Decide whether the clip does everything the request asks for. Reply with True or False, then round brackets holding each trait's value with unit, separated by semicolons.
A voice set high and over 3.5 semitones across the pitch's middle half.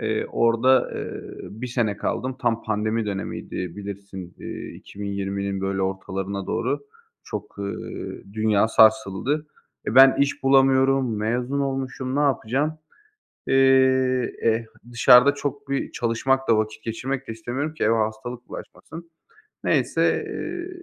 False (120 Hz; 3.9 semitones)